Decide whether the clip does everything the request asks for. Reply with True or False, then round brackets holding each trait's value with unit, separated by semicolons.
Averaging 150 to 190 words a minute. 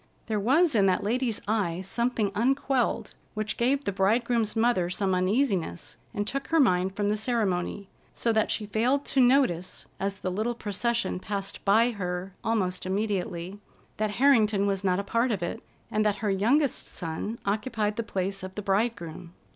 True (170 wpm)